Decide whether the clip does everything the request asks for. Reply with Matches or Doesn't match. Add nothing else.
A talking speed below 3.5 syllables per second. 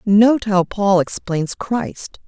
Matches